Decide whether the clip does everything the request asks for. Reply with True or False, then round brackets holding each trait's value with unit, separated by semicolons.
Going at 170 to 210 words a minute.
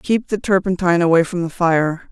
True (200 wpm)